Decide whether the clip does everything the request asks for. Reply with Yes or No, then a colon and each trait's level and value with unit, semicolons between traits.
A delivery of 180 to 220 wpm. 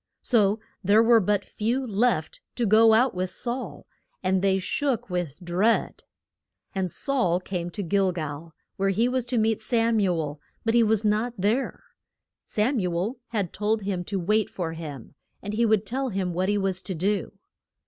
Yes: average, 185 wpm